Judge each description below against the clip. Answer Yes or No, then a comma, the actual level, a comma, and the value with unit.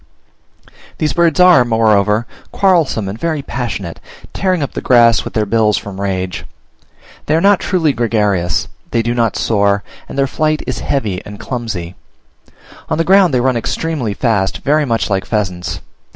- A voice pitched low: Yes, low, 115 Hz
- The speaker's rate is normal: Yes, average, 165 wpm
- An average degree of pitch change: No, wide, 6.9 semitones